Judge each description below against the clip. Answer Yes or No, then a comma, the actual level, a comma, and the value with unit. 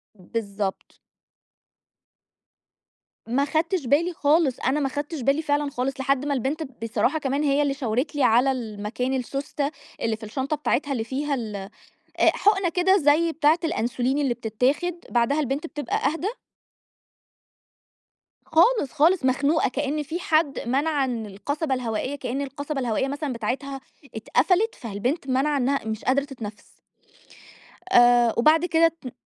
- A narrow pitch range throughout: No, average, 3.7 semitones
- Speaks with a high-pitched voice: Yes, very high, 275 Hz